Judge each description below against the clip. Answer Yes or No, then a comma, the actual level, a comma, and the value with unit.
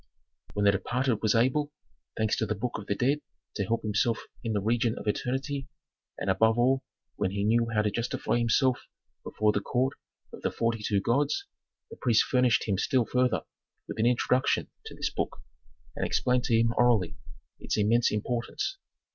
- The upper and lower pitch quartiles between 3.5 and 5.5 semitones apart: No, average, 2.9 semitones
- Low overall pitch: Yes, low, 115 Hz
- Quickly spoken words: No, average, 180 wpm